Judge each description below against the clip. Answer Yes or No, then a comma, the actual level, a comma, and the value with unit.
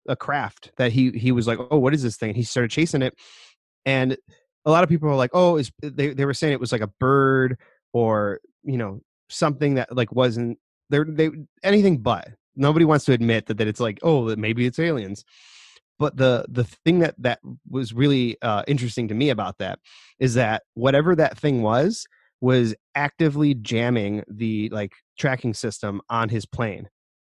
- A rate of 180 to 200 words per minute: Yes, average, 190 wpm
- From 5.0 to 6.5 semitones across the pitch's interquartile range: No, average, 4.1 semitones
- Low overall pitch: Yes, low, 125 Hz